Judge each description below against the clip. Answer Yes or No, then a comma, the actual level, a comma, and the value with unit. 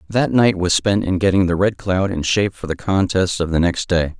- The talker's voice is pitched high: No, very low, 95 Hz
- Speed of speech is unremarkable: No, fast, 260 wpm